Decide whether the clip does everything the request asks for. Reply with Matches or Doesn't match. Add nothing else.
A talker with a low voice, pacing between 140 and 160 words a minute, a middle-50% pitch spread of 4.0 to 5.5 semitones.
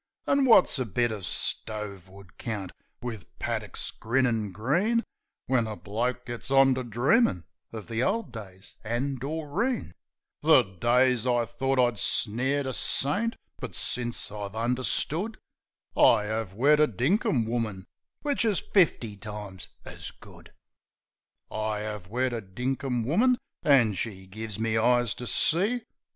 Matches